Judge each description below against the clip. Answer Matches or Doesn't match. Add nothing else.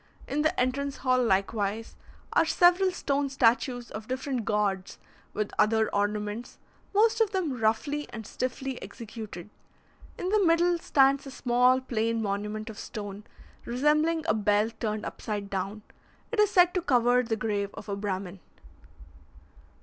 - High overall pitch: Matches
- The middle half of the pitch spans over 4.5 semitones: Matches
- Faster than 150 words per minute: Doesn't match